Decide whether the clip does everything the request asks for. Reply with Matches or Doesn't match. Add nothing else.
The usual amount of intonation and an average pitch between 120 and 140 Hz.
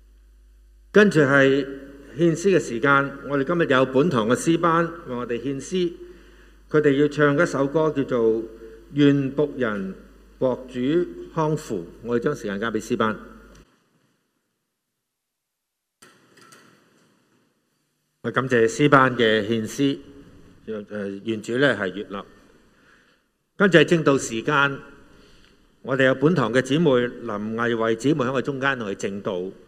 Matches